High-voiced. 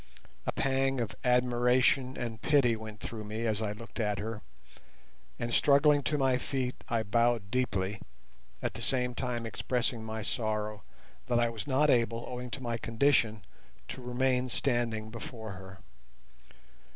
No: low, 120 Hz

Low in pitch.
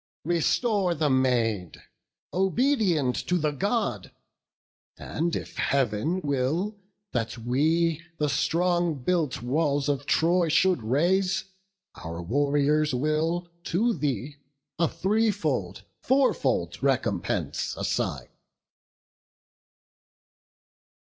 No: medium, 155 Hz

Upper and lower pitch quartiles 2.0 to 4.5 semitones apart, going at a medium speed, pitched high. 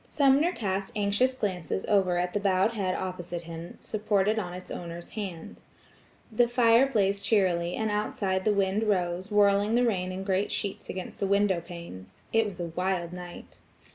Yes: average, 2.9 semitones; average, 170 wpm; high, 195 Hz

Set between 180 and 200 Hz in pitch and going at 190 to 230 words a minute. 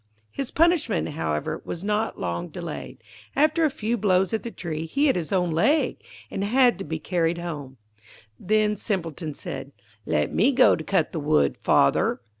No: medium, 185 Hz; average, 175 wpm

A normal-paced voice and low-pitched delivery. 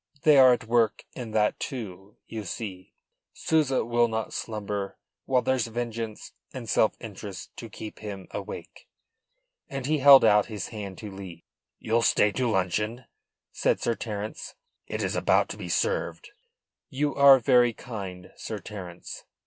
Yes: average, 160 wpm; low, 110 Hz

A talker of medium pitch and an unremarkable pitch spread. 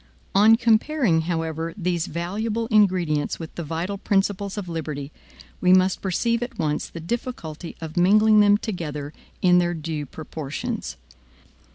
Yes: medium, 180 Hz; average, 4.4 semitones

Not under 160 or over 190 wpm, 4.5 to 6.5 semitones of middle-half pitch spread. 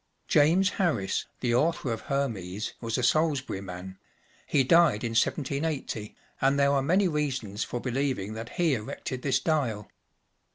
No: average, 150 wpm; average, 5.1 semitones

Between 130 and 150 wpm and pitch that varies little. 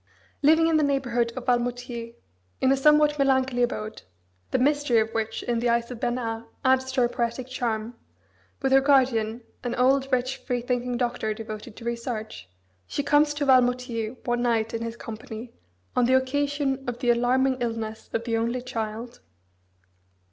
No: average, 165 wpm; narrow, 2.3 semitones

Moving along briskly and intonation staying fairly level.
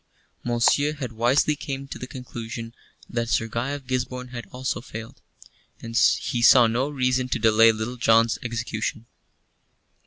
No: average, 150 wpm; narrow, 2.0 semitones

